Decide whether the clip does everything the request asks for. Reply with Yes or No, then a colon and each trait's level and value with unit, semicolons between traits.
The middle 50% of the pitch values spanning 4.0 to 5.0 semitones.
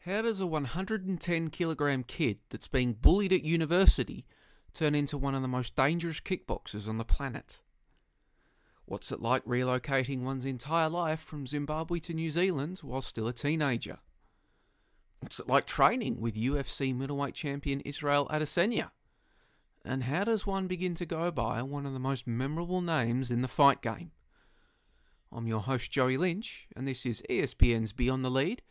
Yes: average, 4.5 semitones